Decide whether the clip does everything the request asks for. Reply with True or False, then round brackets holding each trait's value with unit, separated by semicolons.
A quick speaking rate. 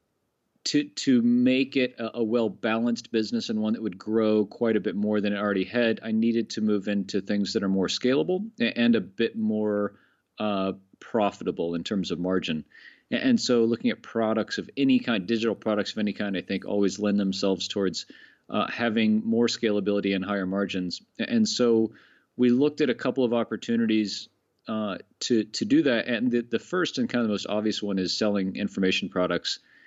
False (195 wpm)